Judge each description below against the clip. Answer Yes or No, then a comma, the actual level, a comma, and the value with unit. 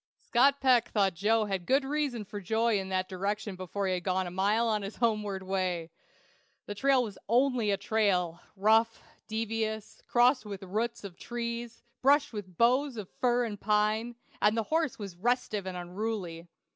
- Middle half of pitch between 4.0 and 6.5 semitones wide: No, average, 3.6 semitones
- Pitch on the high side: Yes, high, 215 Hz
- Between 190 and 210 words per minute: No, average, 175 wpm